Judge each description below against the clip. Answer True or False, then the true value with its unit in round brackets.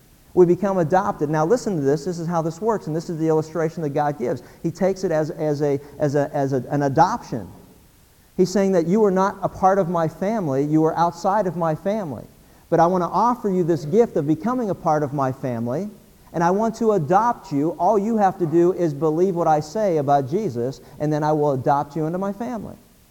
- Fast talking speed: True (235 wpm)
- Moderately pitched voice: True (170 Hz)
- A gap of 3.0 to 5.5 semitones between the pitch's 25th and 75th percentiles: True (4.5 semitones)